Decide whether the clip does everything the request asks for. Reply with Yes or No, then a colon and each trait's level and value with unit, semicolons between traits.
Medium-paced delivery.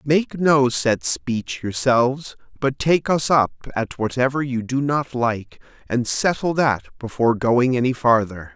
Yes: average, 155 wpm